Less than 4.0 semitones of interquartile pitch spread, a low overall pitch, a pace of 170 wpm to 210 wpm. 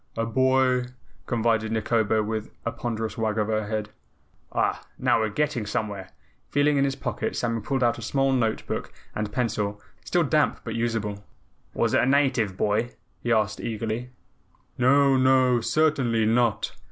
No: average, 3.0 semitones; low, 115 Hz; average, 160 wpm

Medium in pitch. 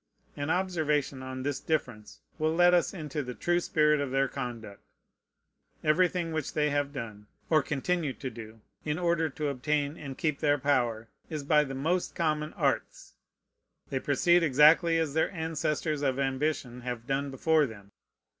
Yes: medium, 145 Hz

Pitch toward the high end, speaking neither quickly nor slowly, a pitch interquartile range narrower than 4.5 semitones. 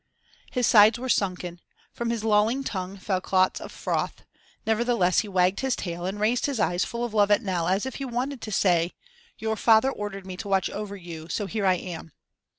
No: high, 205 Hz; fast, 210 wpm; average, 3.8 semitones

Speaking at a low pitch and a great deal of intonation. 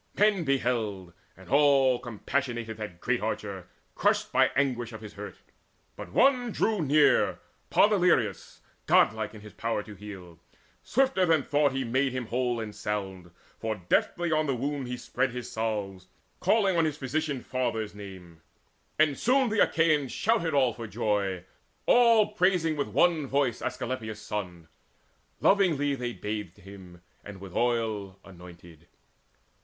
Yes: low, 120 Hz; wide, 6.4 semitones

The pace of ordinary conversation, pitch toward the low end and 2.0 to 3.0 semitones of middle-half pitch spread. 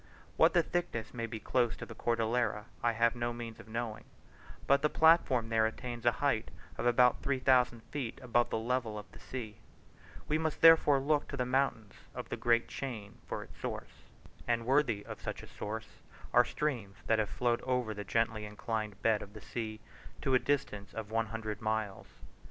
Yes: average, 195 wpm; low, 115 Hz; average, 2.7 semitones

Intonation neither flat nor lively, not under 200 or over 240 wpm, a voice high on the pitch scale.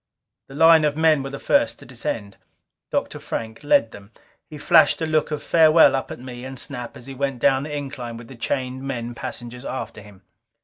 No: average, 3.9 semitones; fast, 205 wpm; low, 135 Hz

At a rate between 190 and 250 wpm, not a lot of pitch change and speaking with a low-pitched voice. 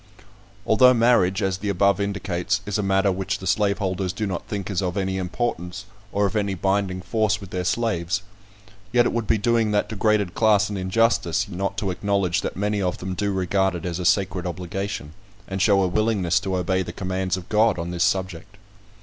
Yes: average, 200 wpm; narrow, 2.1 semitones; very low, 95 Hz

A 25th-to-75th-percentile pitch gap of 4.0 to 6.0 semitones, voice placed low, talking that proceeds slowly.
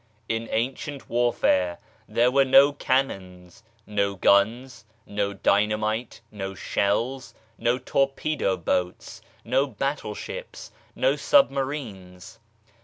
Yes: average, 5.0 semitones; low, 115 Hz; slow, 95 wpm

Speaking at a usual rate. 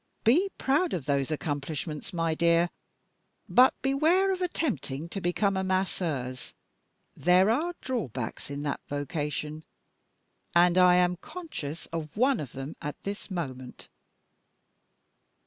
No: slow, 125 wpm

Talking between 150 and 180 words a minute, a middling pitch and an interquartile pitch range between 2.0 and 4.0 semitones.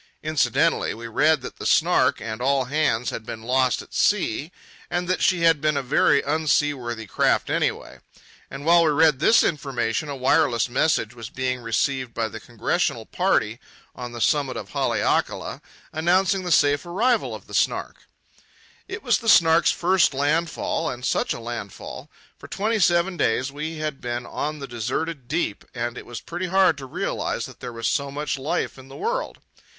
No: average, 175 wpm; medium, 145 Hz; average, 5.3 semitones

